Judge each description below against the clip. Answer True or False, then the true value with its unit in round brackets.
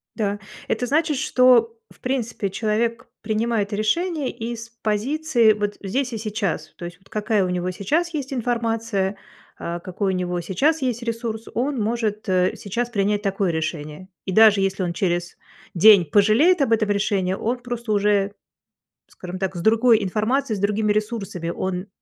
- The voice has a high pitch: True (215 Hz)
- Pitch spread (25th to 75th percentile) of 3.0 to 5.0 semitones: True (3.5 semitones)